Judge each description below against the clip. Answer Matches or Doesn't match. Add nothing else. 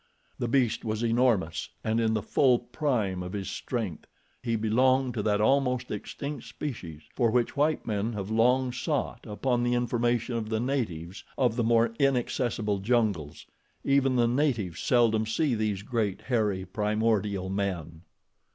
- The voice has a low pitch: Matches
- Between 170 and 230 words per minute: Doesn't match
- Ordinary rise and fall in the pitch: Matches